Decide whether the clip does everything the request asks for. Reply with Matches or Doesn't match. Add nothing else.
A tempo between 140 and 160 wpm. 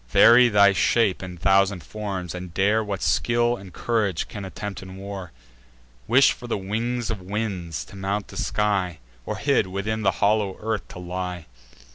Doesn't match